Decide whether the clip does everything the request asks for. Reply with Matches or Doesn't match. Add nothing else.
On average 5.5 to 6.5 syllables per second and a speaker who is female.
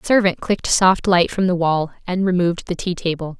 Matches